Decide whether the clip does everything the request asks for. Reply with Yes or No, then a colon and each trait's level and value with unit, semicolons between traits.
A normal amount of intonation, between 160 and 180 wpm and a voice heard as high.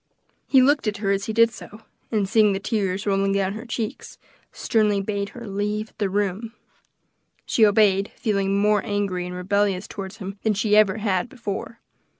No: narrow, 1.8 semitones; average, 175 wpm; high, 205 Hz